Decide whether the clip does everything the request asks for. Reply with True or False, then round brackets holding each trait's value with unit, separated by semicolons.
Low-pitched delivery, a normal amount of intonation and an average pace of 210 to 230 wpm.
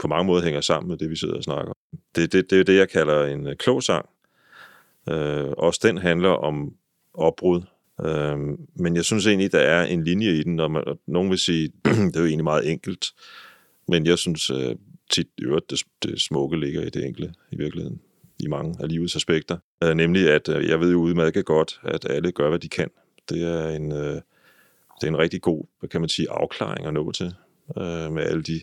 False (80 Hz; 2.1 semitones; 220 wpm)